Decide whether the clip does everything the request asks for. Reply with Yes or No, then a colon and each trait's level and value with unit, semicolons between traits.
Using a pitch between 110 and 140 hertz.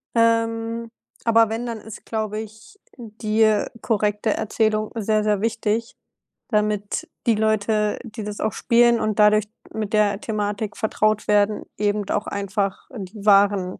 No: high, 215 Hz